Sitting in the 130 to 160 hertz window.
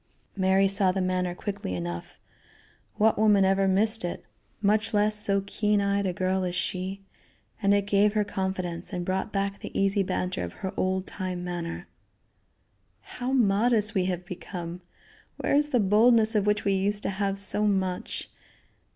No: high, 195 Hz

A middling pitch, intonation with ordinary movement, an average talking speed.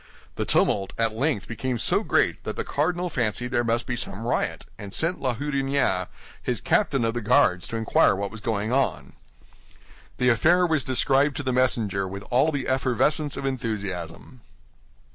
No: low, 125 Hz; average, 4.1 semitones; average, 175 wpm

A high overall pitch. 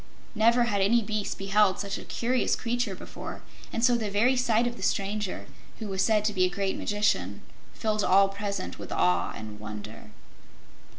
Yes: high, 205 Hz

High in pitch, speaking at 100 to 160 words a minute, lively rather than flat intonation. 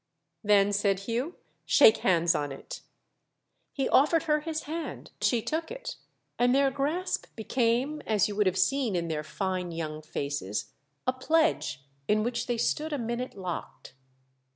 Yes: high, 230 Hz; average, 155 wpm; wide, 7.6 semitones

